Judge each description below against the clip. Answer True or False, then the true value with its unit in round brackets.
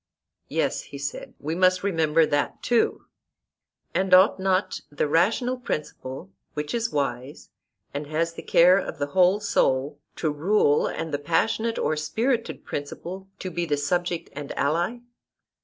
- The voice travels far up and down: False (4.6 semitones)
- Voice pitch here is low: False (165 Hz)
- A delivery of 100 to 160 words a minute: True (150 wpm)